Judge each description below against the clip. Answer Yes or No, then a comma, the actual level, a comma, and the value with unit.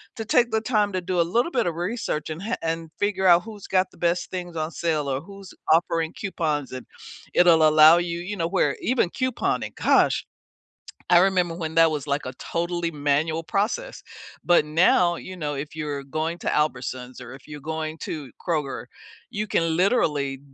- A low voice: No, medium, 165 Hz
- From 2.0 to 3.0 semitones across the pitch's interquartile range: No, average, 3.5 semitones